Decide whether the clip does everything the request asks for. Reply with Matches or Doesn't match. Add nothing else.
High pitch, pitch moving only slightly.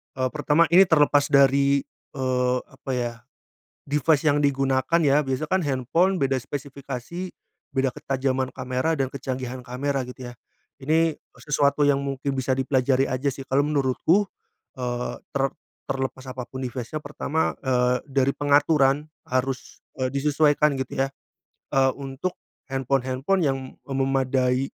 Doesn't match